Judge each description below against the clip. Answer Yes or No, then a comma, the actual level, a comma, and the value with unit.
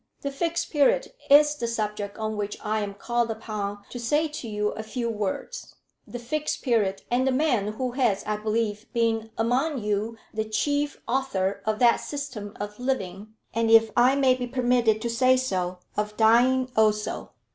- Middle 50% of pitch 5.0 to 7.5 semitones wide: No, average, 3.4 semitones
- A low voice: No, high, 230 Hz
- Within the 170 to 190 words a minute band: Yes, average, 180 wpm